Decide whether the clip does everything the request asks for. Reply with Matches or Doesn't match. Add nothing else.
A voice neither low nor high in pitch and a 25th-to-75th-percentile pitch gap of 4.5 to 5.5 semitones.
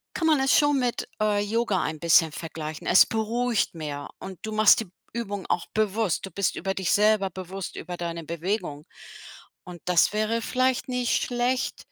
Doesn't match